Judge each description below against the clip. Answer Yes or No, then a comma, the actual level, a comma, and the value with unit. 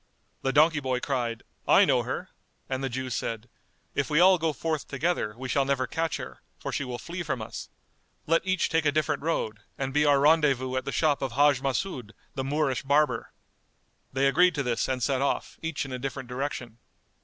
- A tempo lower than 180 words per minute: No, fast, 205 wpm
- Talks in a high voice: No, medium, 140 Hz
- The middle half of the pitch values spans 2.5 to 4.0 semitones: Yes, average, 2.9 semitones